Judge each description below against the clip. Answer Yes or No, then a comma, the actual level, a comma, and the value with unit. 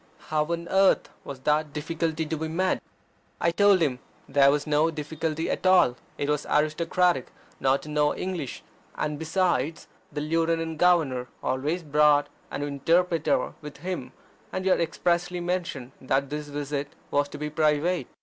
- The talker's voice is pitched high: No, medium, 155 Hz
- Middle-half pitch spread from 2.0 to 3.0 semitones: Yes, average, 2.7 semitones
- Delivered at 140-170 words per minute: Yes, average, 160 wpm